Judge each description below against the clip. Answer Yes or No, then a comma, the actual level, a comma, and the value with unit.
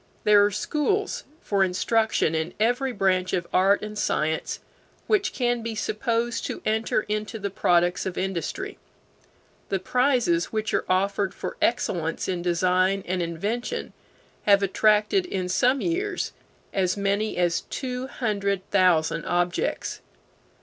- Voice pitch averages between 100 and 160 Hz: No, high, 200 Hz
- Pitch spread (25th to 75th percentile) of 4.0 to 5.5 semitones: Yes, average, 4.3 semitones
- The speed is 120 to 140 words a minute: Yes, slow, 135 wpm